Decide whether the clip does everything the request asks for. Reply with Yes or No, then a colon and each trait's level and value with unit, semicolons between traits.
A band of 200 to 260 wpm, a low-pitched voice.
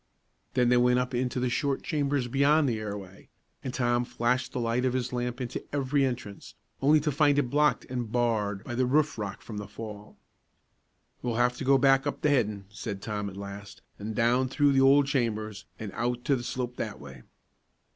Yes: fast, 205 wpm; low, 125 Hz